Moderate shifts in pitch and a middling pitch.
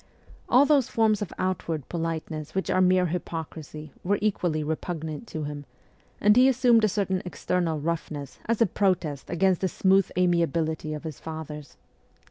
Yes: average, 3.7 semitones; medium, 175 Hz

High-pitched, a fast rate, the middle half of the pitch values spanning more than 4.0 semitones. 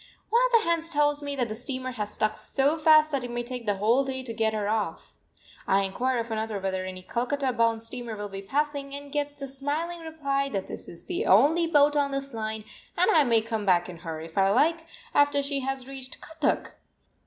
Yes: very high, 260 Hz; fast, 225 wpm; average, 4.9 semitones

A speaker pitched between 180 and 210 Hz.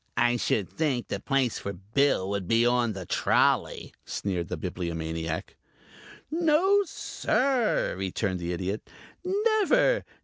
No: low, 115 Hz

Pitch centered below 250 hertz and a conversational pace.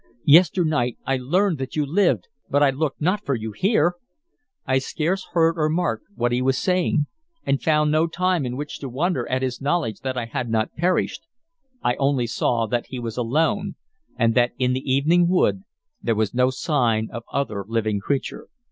Yes: low, 135 Hz; average, 190 wpm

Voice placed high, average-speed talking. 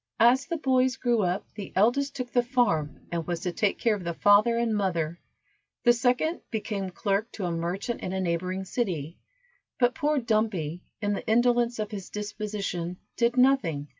Yes: high, 210 Hz; average, 180 wpm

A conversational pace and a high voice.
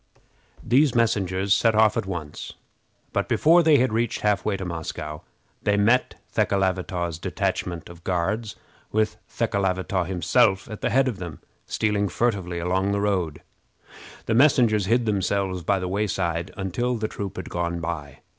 No: average, 155 wpm; low, 100 Hz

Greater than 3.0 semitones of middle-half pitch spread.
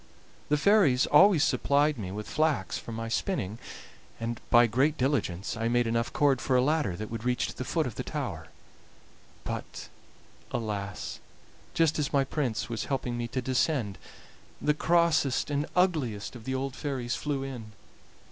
Yes: average, 4.4 semitones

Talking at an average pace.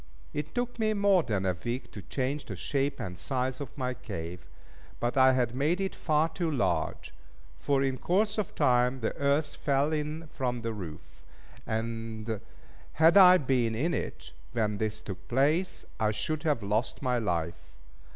Yes: average, 170 wpm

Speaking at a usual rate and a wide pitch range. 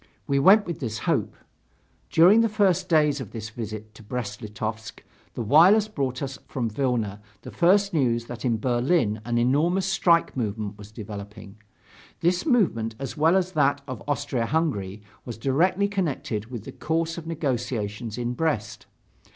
Yes: average, 160 wpm; wide, 7.1 semitones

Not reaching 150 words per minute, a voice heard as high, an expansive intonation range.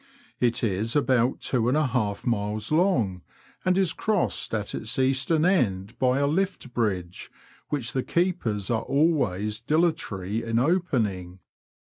No: average, 140 wpm; low, 120 Hz; wide, 6.6 semitones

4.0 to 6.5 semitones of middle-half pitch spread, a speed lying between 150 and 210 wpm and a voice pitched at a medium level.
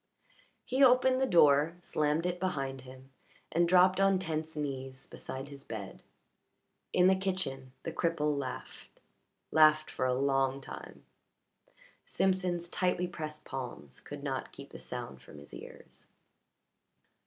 No: average, 5.1 semitones; slow, 135 wpm; medium, 155 Hz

